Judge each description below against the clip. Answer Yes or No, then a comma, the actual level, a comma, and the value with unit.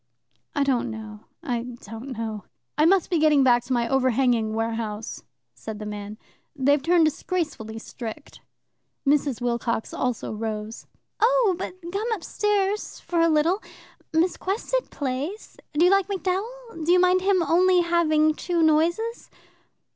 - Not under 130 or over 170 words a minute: Yes, average, 145 wpm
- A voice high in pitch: Yes, very high, 305 Hz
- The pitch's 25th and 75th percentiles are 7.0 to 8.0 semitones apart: Yes, wide, 7.6 semitones